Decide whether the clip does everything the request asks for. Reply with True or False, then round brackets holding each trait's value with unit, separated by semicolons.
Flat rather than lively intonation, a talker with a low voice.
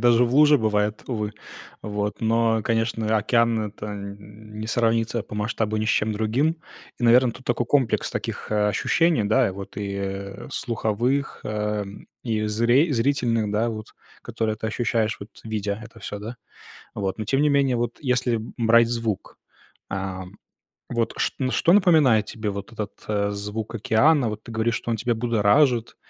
True (2.3 semitones; 110 Hz)